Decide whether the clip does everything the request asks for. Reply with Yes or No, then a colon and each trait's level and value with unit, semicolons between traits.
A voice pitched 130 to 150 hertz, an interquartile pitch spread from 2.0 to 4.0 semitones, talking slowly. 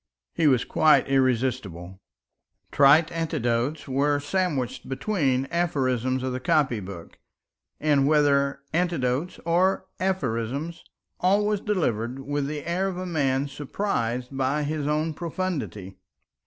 No: medium, 140 Hz; average, 4.5 semitones; slow, 115 wpm